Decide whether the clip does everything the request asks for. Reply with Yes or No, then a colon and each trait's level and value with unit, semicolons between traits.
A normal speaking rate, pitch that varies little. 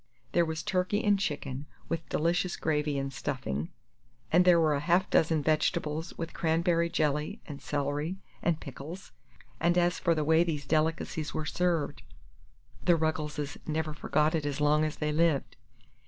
Yes: average, 160 wpm; narrow, 2.3 semitones